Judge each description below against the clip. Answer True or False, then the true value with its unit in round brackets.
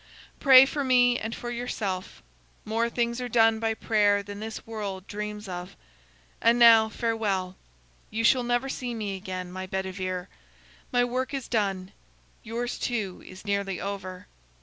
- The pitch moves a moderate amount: True (3.8 semitones)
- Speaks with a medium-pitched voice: False (220 Hz)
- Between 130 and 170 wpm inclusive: True (150 wpm)